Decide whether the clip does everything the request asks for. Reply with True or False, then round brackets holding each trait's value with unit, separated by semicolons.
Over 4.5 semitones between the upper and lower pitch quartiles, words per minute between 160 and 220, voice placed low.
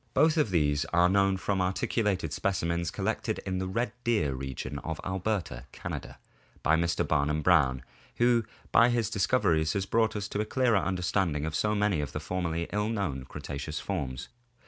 True (5.1 semitones; 180 wpm; 90 Hz)